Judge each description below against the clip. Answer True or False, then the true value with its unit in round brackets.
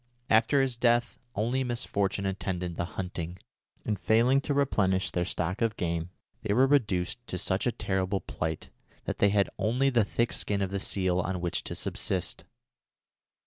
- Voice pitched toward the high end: False (100 Hz)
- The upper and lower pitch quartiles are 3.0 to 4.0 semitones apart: False (4.4 semitones)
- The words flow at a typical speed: True (170 wpm)